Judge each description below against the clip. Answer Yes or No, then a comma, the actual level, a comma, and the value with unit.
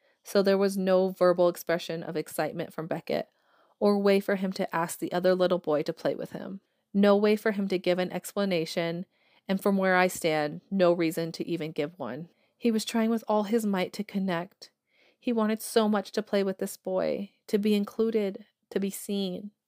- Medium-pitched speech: No, high, 195 Hz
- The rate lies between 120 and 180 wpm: No, fast, 205 wpm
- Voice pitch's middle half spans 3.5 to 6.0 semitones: No, average, 2.8 semitones